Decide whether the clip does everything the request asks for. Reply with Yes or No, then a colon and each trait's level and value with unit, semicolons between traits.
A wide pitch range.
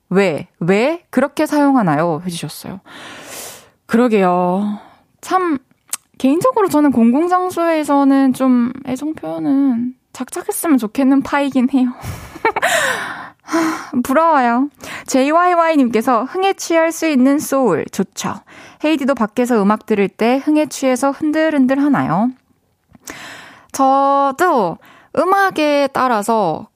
No: average, 4.4 semitones